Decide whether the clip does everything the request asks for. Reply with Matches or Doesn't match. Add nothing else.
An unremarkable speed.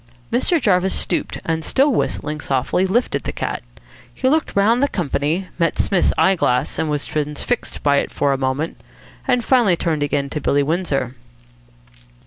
Matches